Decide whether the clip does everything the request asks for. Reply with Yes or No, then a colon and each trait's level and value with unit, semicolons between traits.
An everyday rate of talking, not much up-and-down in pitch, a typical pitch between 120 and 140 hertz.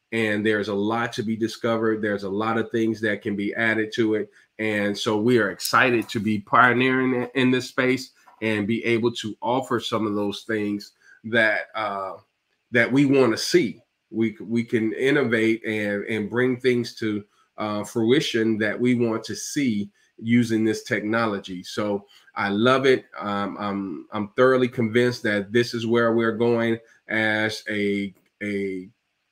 No: average, 170 wpm; narrow, 2.3 semitones; low, 110 Hz